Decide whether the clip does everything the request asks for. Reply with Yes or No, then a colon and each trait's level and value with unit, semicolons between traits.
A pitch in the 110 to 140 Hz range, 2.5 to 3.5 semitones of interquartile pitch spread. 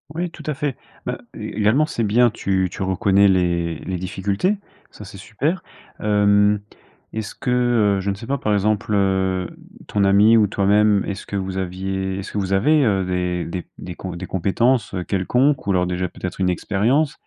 No: low, 100 Hz; average, 2.8 semitones